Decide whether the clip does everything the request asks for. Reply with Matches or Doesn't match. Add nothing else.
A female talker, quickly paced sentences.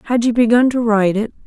Matches